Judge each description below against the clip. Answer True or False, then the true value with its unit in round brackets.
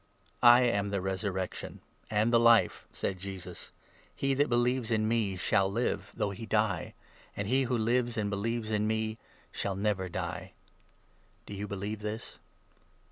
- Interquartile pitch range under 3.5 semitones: True (2.9 semitones)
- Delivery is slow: False (165 wpm)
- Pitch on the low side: True (110 Hz)